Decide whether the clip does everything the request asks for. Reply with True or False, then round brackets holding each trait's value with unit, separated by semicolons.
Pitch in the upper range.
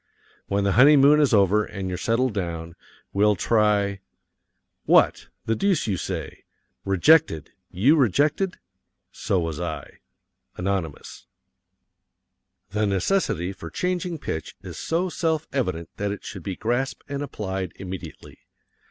False (105 Hz)